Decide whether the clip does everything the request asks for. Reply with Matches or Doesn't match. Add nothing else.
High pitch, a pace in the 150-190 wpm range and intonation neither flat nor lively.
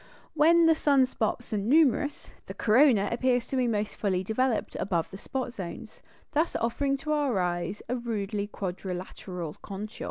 Doesn't match